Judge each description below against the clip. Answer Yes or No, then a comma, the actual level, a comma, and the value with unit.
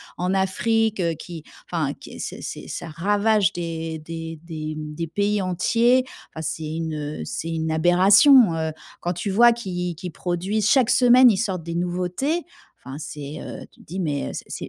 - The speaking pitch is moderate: Yes, medium, 175 Hz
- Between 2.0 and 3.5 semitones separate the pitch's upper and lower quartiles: No, average, 4.3 semitones